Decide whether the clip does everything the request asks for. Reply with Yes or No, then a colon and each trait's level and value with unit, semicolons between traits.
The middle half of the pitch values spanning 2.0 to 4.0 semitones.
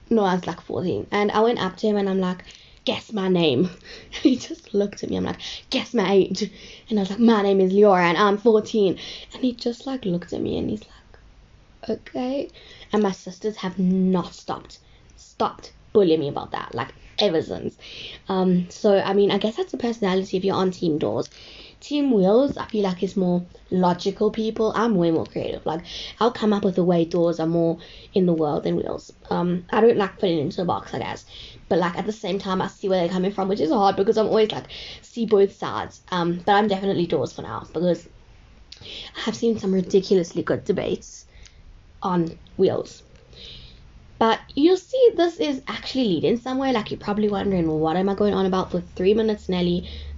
Yes: average, 3.4 semitones